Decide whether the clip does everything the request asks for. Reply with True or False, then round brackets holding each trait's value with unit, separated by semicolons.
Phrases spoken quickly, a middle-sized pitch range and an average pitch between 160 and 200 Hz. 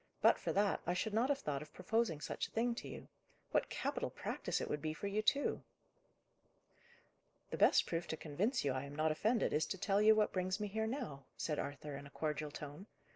False (225 wpm; 6.4 semitones; 185 Hz)